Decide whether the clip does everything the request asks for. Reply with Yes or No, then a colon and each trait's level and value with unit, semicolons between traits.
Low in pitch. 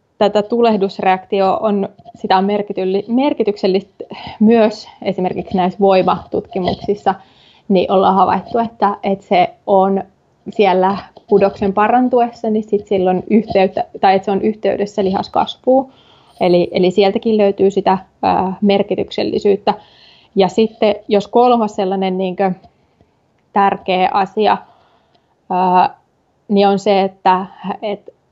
No: high, 200 Hz